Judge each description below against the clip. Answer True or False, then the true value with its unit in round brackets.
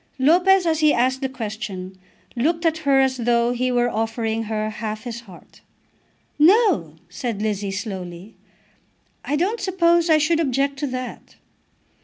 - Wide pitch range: True (6.3 semitones)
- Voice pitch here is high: True (250 Hz)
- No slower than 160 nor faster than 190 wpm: False (150 wpm)